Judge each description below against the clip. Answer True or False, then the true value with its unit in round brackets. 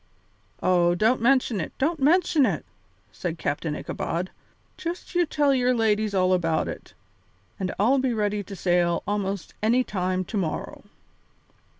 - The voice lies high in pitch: True (210 Hz)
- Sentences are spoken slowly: False (145 wpm)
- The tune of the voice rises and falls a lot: True (6.0 semitones)